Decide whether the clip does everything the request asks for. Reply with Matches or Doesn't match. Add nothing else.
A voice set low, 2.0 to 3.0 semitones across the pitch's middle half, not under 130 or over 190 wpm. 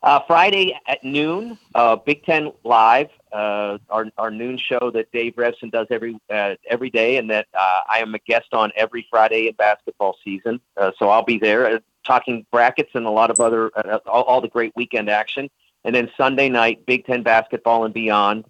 Doesn't match